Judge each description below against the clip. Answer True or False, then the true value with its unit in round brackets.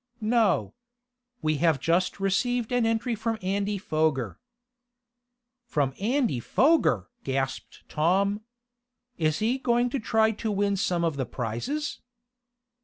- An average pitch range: False (6.7 semitones)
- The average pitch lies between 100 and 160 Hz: False (200 Hz)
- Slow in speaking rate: True (120 wpm)